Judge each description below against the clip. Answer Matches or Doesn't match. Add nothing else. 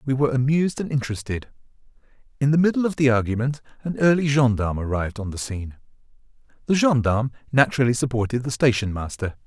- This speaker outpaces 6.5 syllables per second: Matches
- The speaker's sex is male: Matches